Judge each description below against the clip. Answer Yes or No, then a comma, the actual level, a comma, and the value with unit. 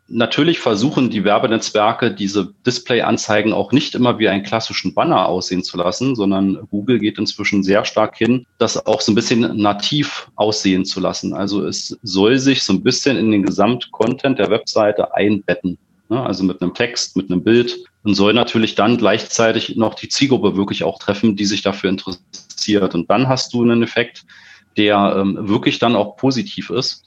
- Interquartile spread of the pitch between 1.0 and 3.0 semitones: No, average, 3.5 semitones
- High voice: No, low, 105 Hz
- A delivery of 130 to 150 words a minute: No, average, 175 wpm